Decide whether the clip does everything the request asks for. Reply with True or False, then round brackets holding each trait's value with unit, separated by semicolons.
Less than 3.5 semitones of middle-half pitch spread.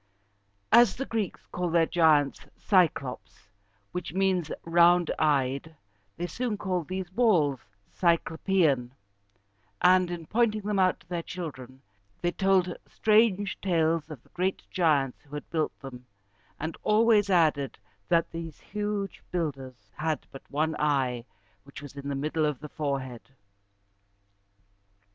False (4.5 semitones)